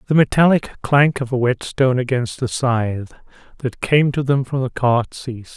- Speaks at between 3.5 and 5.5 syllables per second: Yes, 4.9 syllables/s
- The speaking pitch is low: Yes, low, 130 Hz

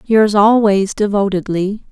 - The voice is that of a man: No, female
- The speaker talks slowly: Yes, slow, 95 wpm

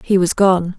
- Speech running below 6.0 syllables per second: Yes, 4.4 syllables/s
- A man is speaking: No, female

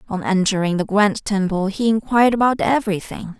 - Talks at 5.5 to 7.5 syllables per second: Yes, 5.6 syllables/s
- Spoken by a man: No, female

